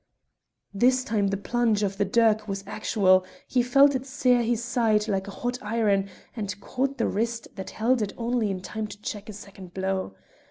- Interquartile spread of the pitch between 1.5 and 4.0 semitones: Yes, average, 3.3 semitones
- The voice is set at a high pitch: Yes, high, 215 Hz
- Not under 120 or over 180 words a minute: No, average, 195 wpm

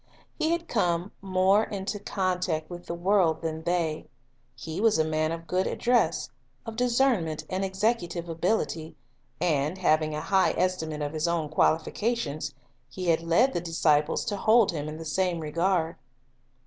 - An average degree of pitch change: Yes, average, 3.5 semitones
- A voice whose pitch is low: No, medium, 175 Hz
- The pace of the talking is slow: No, average, 160 wpm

